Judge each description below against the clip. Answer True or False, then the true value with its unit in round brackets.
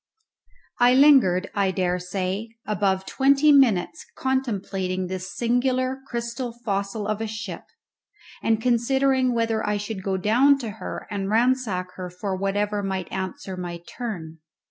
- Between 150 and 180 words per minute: False (135 wpm)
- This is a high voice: True (210 Hz)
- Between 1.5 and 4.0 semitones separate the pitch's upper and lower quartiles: False (4.6 semitones)